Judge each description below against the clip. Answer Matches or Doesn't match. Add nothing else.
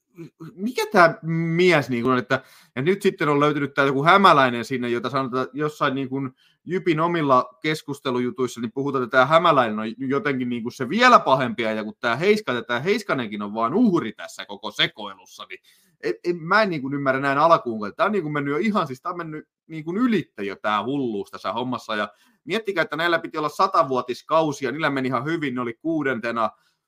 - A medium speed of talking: Doesn't match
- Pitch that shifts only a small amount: Doesn't match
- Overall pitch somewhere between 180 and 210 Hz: Doesn't match